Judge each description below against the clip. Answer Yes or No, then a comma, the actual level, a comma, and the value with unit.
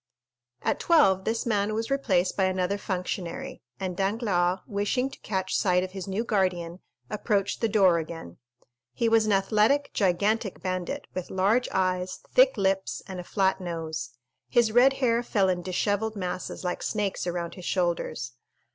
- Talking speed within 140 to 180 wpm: Yes, average, 160 wpm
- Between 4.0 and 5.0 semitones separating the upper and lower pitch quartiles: No, average, 3.3 semitones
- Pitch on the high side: Yes, high, 195 Hz